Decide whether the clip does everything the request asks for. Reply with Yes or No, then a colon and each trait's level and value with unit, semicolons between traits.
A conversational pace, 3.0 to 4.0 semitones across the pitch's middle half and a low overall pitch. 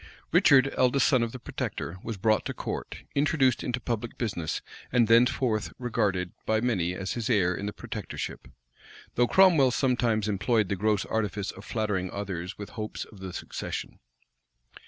Yes: average, 160 wpm; average, 3.6 semitones; low, 110 Hz